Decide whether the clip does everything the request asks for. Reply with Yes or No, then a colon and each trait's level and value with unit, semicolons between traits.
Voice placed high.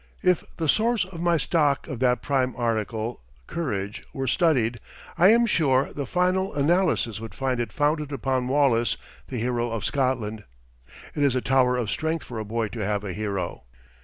No: low, 130 Hz